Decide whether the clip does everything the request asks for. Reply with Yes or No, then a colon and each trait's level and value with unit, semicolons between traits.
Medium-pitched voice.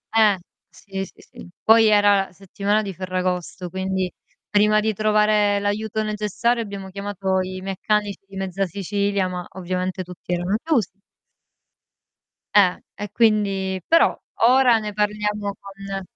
No: high, 200 Hz